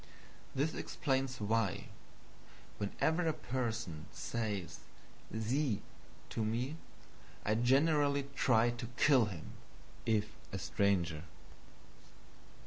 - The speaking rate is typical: No, slow, 90 wpm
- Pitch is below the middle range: Yes, low, 115 Hz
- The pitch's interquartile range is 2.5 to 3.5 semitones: No, average, 4.5 semitones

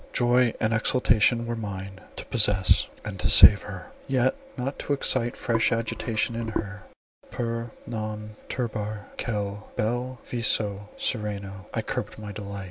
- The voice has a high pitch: No, low, 110 Hz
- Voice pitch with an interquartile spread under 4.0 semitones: Yes, narrow, 2.6 semitones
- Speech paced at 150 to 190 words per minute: No, average, 140 wpm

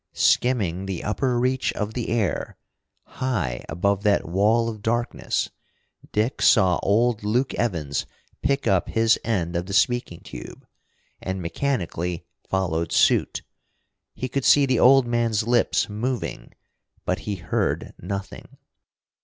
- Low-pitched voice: Yes, low, 105 Hz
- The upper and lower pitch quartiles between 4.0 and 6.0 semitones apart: Yes, average, 4.8 semitones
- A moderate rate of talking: No, slow, 130 wpm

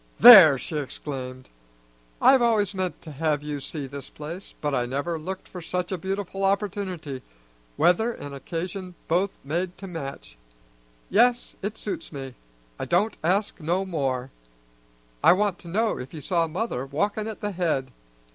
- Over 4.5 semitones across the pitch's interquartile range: Yes, wide, 5.4 semitones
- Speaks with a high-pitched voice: No, medium, 175 Hz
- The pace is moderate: Yes, average, 160 wpm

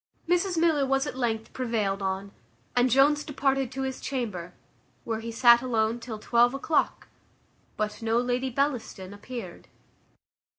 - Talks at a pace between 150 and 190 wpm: No, average, 140 wpm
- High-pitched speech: Yes, high, 245 Hz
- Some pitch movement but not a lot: Yes, average, 3.5 semitones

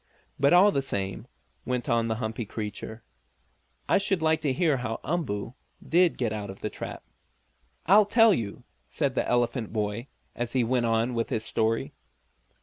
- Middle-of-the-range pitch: No, low, 120 Hz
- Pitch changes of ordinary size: No, wide, 6.1 semitones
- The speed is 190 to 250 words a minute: No, average, 170 wpm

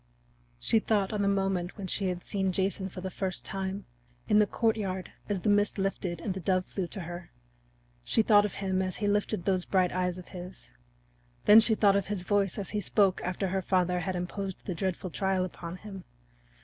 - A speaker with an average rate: No, fast, 210 wpm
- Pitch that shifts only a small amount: Yes, narrow, 1.9 semitones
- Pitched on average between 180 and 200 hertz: Yes, high, 190 Hz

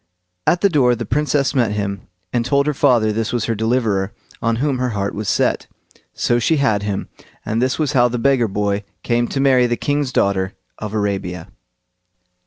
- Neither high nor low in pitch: No, low, 120 Hz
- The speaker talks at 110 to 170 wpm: No, average, 195 wpm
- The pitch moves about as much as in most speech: Yes, average, 4.3 semitones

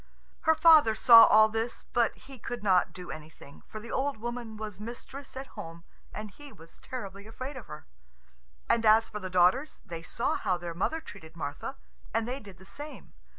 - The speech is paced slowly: No, average, 195 wpm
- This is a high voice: Yes, high, 220 Hz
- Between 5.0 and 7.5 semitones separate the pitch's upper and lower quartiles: Yes, wide, 5.5 semitones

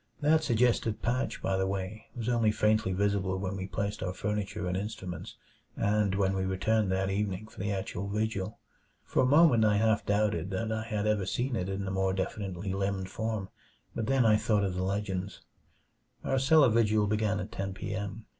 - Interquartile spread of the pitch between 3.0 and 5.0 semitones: No, narrow, 2.5 semitones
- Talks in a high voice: No, low, 105 Hz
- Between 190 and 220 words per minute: Yes, average, 195 wpm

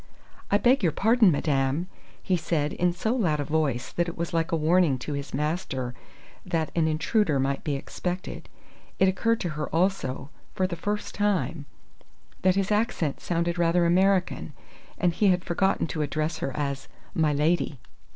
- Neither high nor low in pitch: Yes, medium, 170 Hz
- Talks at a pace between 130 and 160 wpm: No, average, 170 wpm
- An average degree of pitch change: Yes, average, 3.8 semitones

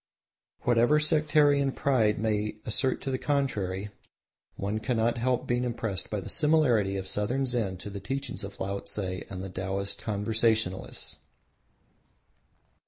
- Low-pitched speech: Yes, low, 110 Hz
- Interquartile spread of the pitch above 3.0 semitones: Yes, average, 4.8 semitones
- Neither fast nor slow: No, slow, 130 wpm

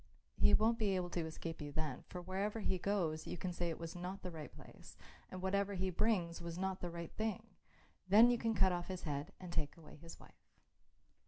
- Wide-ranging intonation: No, average, 3.0 semitones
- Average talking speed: No, fast, 225 wpm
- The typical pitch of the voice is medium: Yes, medium, 180 Hz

